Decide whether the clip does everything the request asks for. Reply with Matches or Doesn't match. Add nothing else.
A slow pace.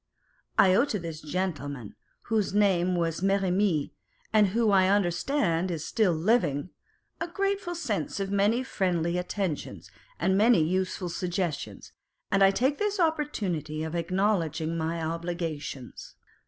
Matches